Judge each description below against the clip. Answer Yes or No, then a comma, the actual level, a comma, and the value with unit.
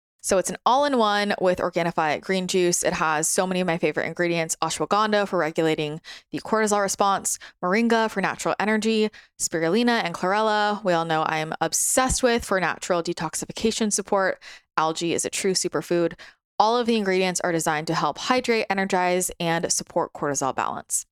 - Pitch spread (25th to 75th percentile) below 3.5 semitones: No, average, 4.3 semitones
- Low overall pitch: No, medium, 185 Hz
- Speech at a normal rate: Yes, average, 170 wpm